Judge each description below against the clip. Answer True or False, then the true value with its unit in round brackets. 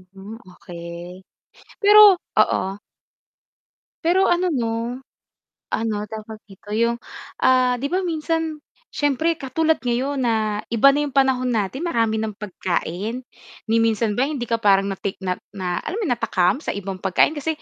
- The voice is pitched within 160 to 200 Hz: False (230 Hz)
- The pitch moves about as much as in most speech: False (5.8 semitones)